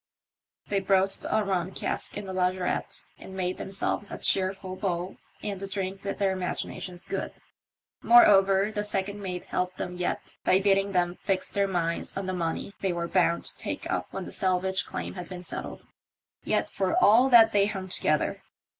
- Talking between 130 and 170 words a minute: No, average, 180 wpm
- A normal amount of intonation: No, narrow, 1.5 semitones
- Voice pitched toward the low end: No, high, 190 Hz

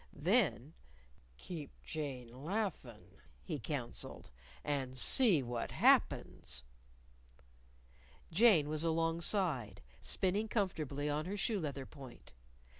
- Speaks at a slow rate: Yes, slow, 100 wpm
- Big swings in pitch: Yes, wide, 6.1 semitones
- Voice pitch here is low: No, medium, 155 Hz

